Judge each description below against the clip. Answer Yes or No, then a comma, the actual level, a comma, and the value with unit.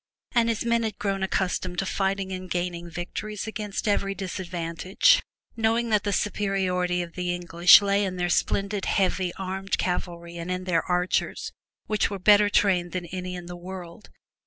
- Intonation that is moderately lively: No, narrow, 2.3 semitones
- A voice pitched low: No, high, 190 Hz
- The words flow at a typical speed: Yes, average, 170 wpm